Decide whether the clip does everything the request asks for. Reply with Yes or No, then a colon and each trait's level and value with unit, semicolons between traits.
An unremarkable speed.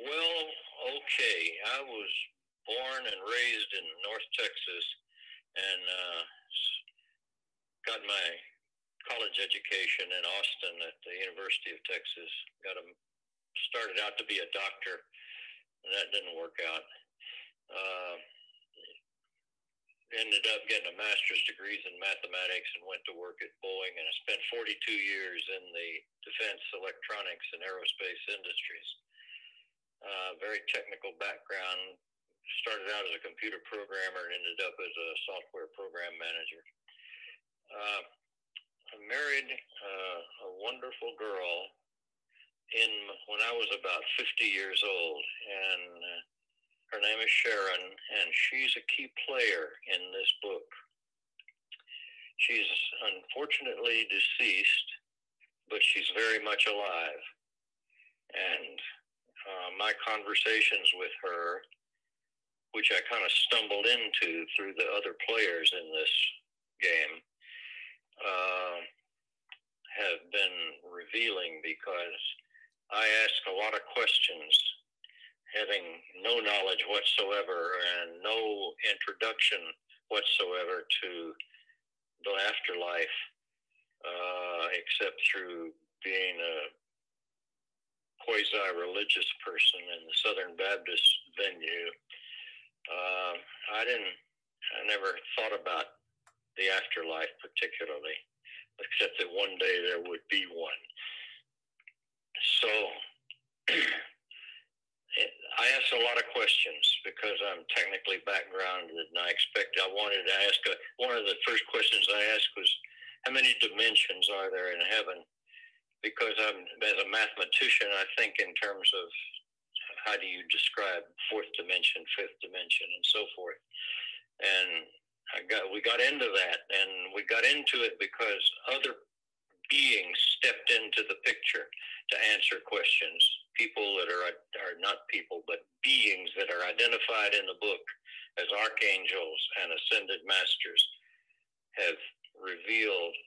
No: slow, 120 wpm